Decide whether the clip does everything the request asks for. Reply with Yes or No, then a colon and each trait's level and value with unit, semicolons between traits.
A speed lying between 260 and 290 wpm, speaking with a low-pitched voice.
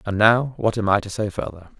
Yes: fast, 265 wpm; low, 105 Hz